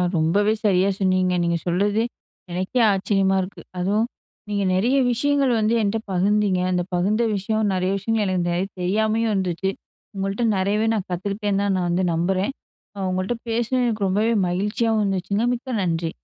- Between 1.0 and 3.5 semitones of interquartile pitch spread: Yes, average, 2.9 semitones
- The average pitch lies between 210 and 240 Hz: No, high, 200 Hz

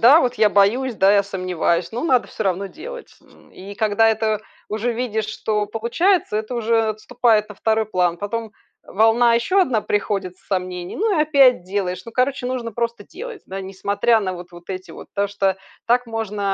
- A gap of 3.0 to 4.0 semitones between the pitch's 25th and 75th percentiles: Yes, average, 3.4 semitones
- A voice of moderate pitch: No, high, 220 Hz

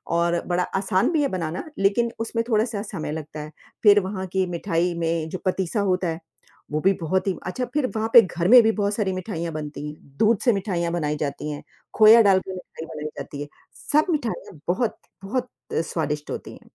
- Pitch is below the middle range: No, medium, 185 Hz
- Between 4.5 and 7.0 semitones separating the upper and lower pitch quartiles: Yes, average, 5.1 semitones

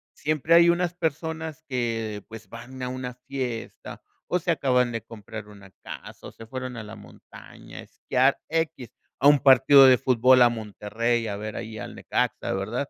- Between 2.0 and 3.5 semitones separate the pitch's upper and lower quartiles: No, average, 4.0 semitones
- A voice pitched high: No, low, 125 Hz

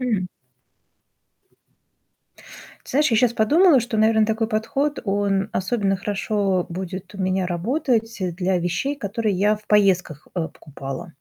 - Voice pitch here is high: Yes, high, 205 Hz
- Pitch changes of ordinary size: Yes, average, 3.4 semitones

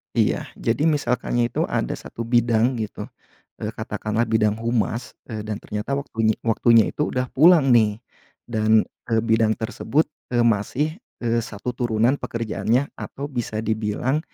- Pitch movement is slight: Yes, narrow, 2.3 semitones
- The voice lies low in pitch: Yes, low, 115 Hz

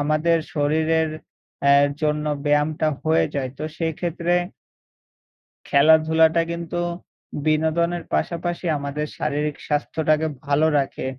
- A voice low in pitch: No, medium, 155 Hz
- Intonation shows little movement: Yes, narrow, 1.6 semitones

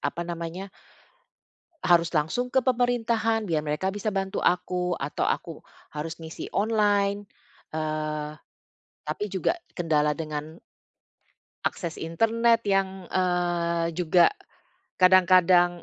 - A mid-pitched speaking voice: Yes, medium, 180 Hz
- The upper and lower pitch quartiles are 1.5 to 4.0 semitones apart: Yes, average, 3.7 semitones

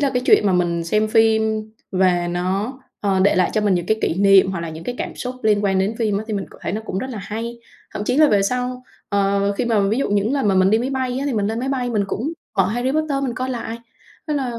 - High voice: Yes, high, 215 Hz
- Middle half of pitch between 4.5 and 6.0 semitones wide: No, average, 4.1 semitones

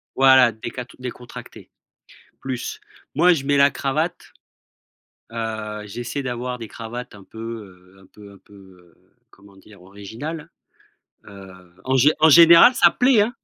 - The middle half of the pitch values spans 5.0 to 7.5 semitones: Yes, wide, 5.5 semitones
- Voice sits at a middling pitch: No, low, 120 Hz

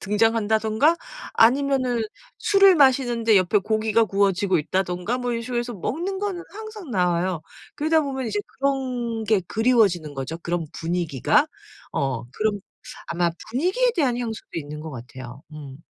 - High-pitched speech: Yes, high, 220 Hz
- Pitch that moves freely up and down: Yes, wide, 7.0 semitones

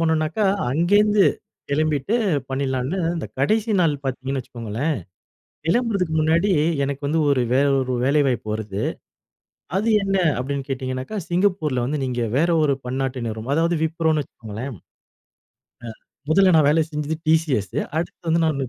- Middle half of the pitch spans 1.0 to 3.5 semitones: No, average, 4.3 semitones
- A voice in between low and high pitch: Yes, medium, 150 Hz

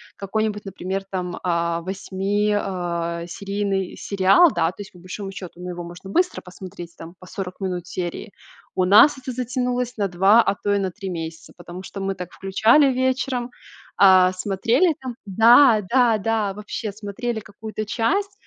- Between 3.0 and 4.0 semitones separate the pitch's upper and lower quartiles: Yes, average, 3.7 semitones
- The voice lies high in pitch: Yes, high, 195 Hz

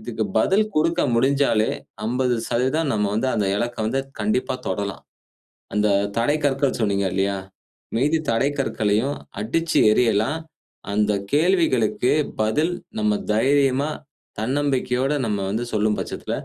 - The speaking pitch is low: Yes, low, 120 Hz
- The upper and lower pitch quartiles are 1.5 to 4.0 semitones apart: No, average, 4.7 semitones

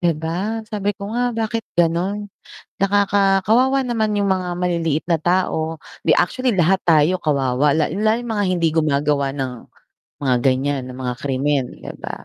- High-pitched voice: No, medium, 175 Hz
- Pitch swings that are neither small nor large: No, wide, 5.7 semitones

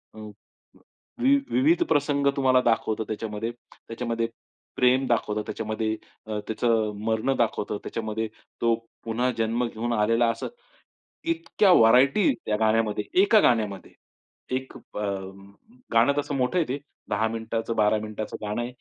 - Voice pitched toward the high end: No, low, 115 Hz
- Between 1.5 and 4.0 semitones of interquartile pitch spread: Yes, average, 2.9 semitones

